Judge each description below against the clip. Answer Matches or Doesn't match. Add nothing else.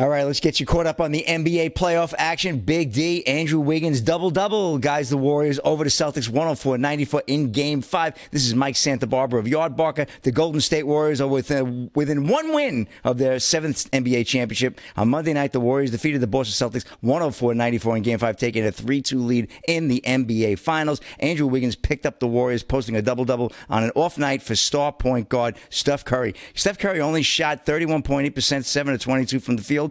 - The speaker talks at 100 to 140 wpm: Doesn't match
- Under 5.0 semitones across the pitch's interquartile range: Matches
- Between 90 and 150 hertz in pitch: Matches